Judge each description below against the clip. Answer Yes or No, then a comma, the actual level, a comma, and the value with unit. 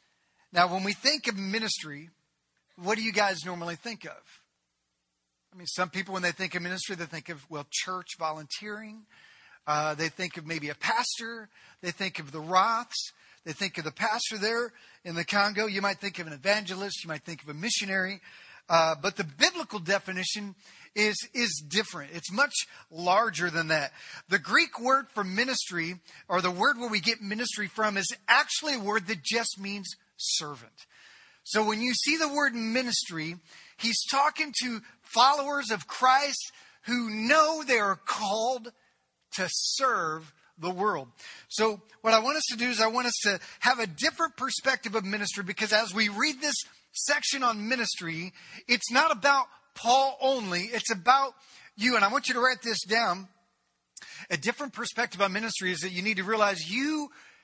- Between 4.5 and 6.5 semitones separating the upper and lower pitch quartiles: Yes, average, 5.2 semitones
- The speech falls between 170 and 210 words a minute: Yes, average, 180 wpm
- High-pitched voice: Yes, high, 210 Hz